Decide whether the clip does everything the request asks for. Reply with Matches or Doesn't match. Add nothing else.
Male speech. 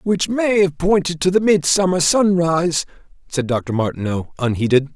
Matches